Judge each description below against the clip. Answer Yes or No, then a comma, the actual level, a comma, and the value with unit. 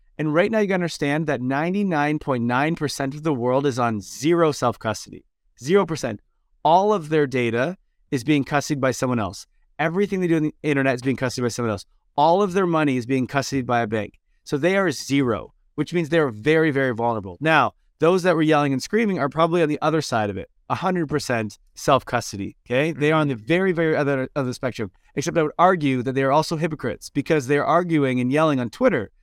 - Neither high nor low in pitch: Yes, medium, 145 Hz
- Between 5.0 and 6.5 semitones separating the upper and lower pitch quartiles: No, average, 4.2 semitones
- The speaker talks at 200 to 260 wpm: Yes, fast, 205 wpm